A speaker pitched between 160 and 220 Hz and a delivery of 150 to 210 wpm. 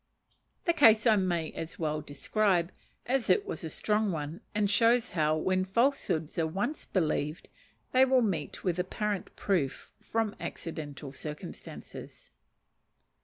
No: medium, 185 Hz; slow, 135 wpm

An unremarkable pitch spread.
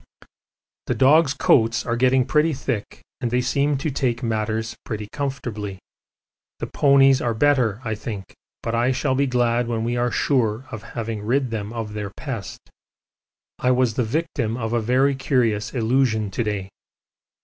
Yes: average, 3.1 semitones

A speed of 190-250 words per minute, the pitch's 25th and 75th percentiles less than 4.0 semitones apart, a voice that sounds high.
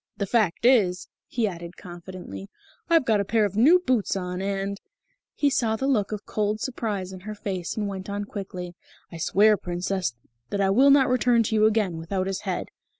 Yes: fast, 205 wpm; average, 3.3 semitones; high, 200 Hz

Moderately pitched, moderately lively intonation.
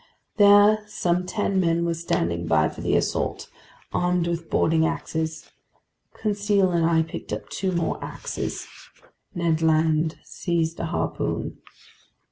No: medium, 170 Hz; narrow, 2.3 semitones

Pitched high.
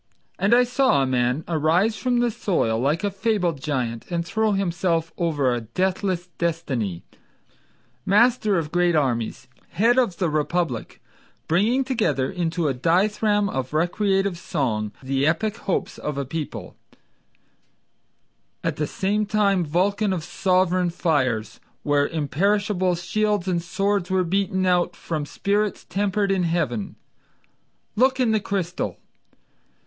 No: medium, 175 Hz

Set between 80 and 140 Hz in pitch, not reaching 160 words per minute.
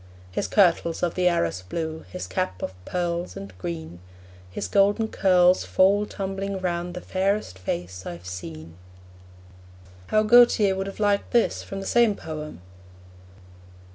No: medium, 175 Hz; average, 140 wpm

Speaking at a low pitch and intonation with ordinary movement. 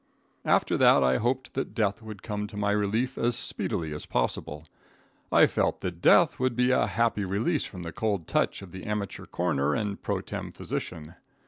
Yes: low, 100 Hz; average, 4.7 semitones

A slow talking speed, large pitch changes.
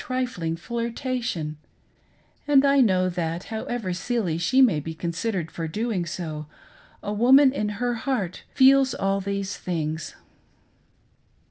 Yes: slow, 125 wpm; wide, 6.4 semitones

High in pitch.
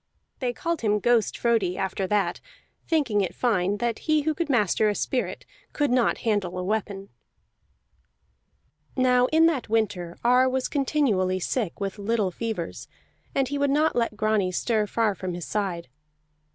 Yes: high, 220 Hz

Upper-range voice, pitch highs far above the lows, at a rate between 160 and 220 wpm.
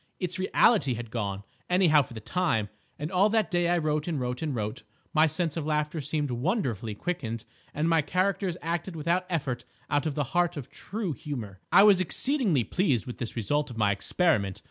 No: medium, 150 Hz; wide, 6.5 semitones; average, 195 wpm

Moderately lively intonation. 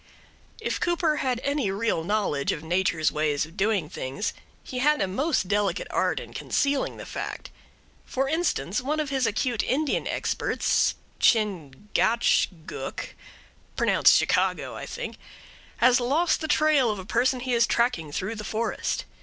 No: wide, 6.4 semitones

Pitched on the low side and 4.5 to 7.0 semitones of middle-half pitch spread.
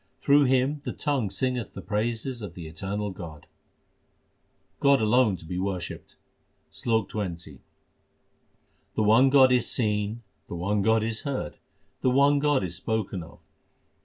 Yes: low, 110 Hz; average, 5.2 semitones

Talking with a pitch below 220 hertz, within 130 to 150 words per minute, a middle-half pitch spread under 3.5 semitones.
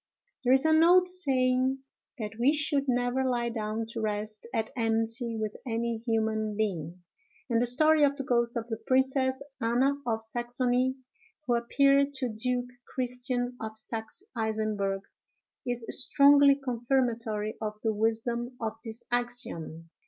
No: high, 240 Hz; average, 145 wpm; average, 2.8 semitones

